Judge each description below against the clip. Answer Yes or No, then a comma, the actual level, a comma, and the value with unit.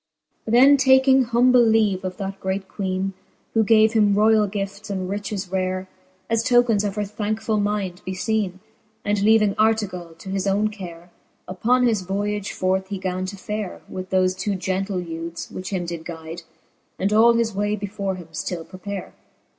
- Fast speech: No, average, 170 wpm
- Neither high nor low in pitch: No, high, 200 Hz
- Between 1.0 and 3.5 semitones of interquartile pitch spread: Yes, narrow, 2.6 semitones